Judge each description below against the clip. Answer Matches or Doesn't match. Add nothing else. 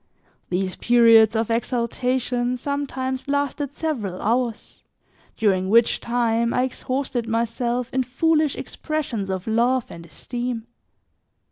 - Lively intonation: Doesn't match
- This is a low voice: Doesn't match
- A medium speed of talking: Doesn't match